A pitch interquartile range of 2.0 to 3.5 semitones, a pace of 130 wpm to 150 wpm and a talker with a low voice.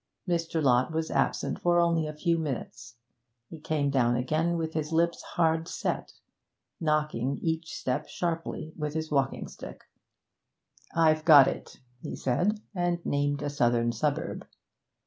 No: average, 2.8 semitones; average, 145 wpm; medium, 155 Hz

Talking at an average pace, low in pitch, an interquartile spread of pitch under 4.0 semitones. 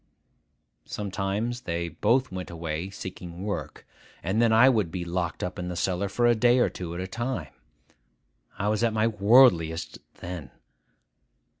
No: average, 160 wpm; very low, 95 Hz; average, 4.7 semitones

